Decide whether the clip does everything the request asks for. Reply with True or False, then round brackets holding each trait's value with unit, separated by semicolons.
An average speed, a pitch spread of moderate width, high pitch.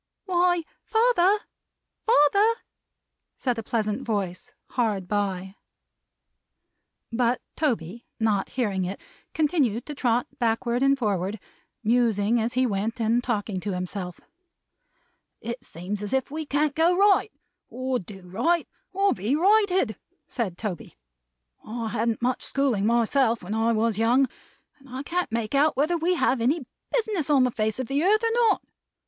False (145 wpm; 5.8 semitones; 240 Hz)